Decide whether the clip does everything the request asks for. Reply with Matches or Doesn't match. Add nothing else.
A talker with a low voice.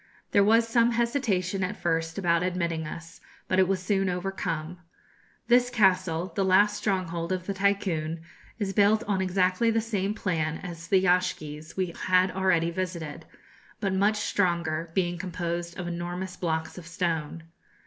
Doesn't match